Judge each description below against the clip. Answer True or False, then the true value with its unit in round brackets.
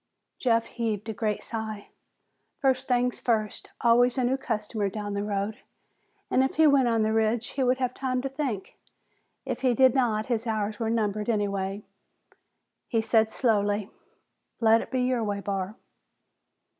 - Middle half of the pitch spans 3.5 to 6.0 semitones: False (3.0 semitones)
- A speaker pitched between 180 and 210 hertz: False (225 Hz)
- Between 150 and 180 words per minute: True (165 wpm)